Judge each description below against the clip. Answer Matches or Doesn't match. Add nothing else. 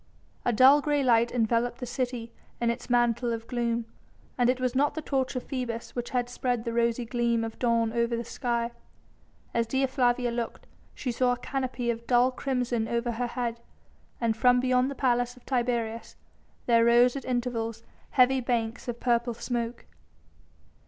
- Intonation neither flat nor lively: Doesn't match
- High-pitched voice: Matches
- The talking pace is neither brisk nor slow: Matches